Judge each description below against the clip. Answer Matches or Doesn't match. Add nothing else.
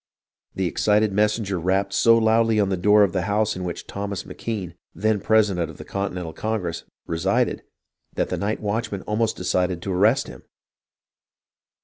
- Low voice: Matches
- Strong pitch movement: Doesn't match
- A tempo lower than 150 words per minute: Doesn't match